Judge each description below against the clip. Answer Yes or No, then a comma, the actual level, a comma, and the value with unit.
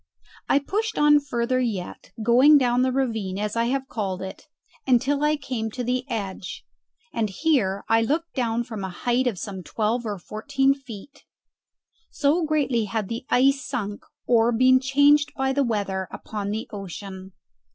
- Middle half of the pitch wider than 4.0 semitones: Yes, average, 4.5 semitones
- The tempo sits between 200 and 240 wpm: No, average, 165 wpm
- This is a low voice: No, high, 240 Hz